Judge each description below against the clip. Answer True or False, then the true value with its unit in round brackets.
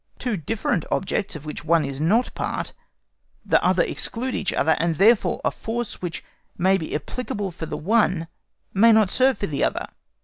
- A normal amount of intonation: False (5.7 semitones)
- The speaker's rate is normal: True (180 wpm)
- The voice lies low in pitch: False (190 Hz)